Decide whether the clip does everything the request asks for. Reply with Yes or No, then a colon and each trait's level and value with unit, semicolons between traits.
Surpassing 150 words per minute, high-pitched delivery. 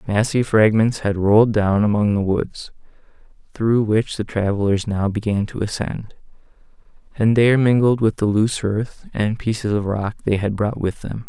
No: average, 170 wpm; low, 105 Hz